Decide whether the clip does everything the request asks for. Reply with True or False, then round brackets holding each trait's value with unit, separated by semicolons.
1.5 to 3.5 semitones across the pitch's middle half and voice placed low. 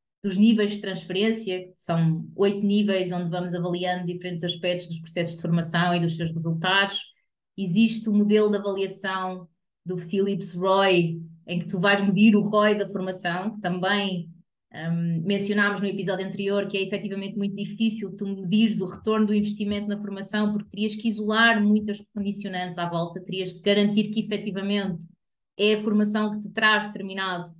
False (2.5 semitones; 195 Hz)